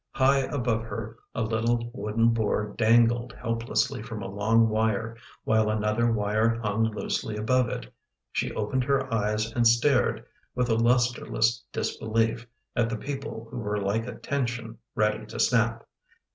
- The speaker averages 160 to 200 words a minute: No, average, 150 wpm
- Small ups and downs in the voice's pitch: Yes, narrow, 1.7 semitones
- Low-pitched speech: Yes, low, 115 Hz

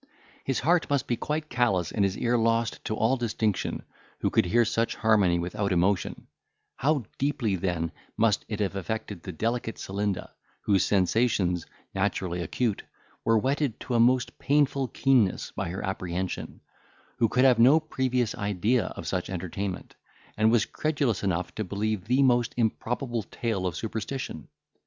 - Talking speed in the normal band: Yes, average, 155 wpm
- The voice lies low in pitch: Yes, low, 110 Hz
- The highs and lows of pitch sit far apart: No, average, 4.4 semitones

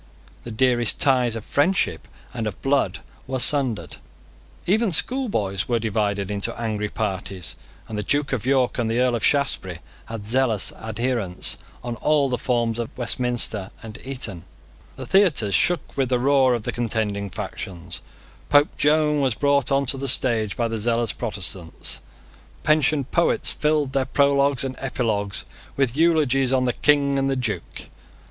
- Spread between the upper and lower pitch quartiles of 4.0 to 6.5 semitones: Yes, average, 4.3 semitones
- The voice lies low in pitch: Yes, low, 125 Hz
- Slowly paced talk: No, average, 155 wpm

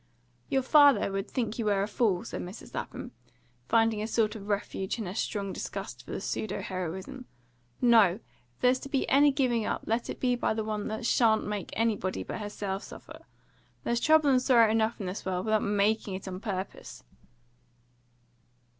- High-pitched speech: Yes, high, 220 Hz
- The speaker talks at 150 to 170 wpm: No, average, 185 wpm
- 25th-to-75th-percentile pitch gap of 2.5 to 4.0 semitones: Yes, average, 3.2 semitones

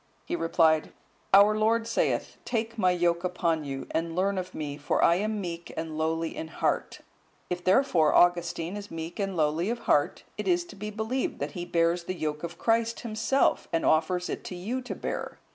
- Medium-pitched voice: Yes, medium, 180 Hz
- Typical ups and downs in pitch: Yes, average, 4.6 semitones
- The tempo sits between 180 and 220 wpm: Yes, average, 195 wpm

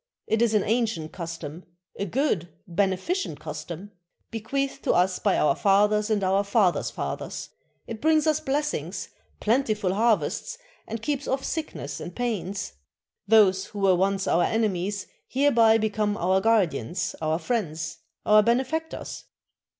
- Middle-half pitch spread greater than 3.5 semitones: Yes, average, 4.1 semitones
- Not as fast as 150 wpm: Yes, slow, 135 wpm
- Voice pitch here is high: Yes, high, 210 Hz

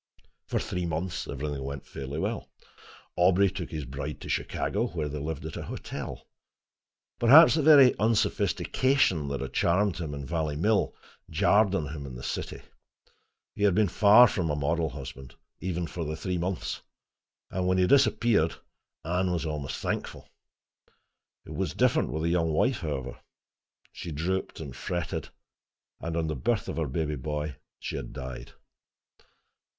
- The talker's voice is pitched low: Yes, very low, 85 Hz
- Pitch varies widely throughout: No, average, 4.2 semitones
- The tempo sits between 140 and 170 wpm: Yes, average, 160 wpm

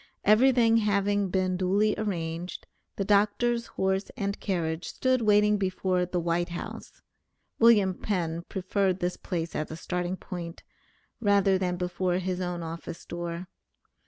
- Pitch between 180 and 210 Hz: Yes, medium, 185 Hz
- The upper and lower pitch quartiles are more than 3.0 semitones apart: No, narrow, 2.6 semitones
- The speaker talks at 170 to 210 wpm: No, slow, 135 wpm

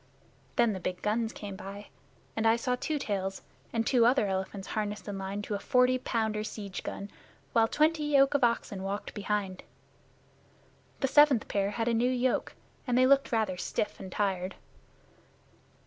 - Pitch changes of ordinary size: Yes, average, 3.9 semitones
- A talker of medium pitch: No, high, 220 Hz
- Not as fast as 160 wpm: No, average, 170 wpm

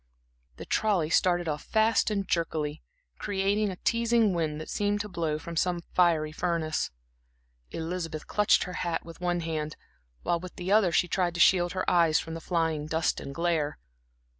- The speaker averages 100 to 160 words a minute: No, average, 175 wpm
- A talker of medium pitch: Yes, medium, 175 Hz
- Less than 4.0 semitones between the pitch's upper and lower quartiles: Yes, narrow, 2.6 semitones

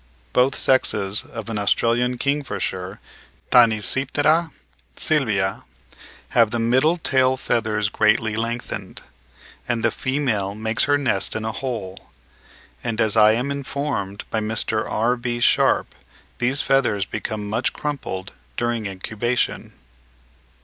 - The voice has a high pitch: No, low, 115 Hz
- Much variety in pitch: No, average, 3.5 semitones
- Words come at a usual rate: No, slow, 115 wpm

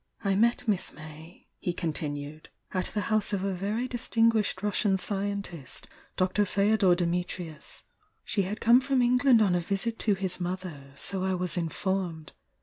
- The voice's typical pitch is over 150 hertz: Yes, high, 190 Hz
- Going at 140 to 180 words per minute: Yes, average, 155 wpm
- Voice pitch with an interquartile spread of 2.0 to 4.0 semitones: Yes, average, 3.3 semitones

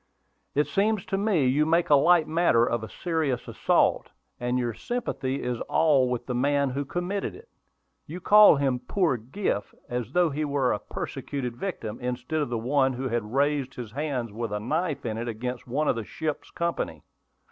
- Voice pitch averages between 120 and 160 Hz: Yes, low, 135 Hz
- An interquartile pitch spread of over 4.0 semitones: Yes, average, 4.8 semitones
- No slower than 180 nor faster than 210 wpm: Yes, average, 190 wpm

